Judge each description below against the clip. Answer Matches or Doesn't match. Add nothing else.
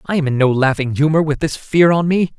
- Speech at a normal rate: Doesn't match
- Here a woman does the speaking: Doesn't match